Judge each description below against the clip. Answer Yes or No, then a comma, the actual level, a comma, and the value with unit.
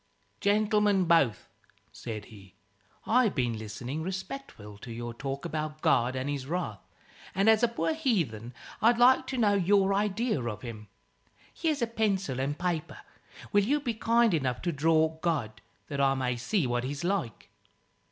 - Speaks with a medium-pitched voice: Yes, medium, 160 Hz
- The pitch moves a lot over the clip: Yes, wide, 8.9 semitones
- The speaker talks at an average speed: Yes, average, 160 wpm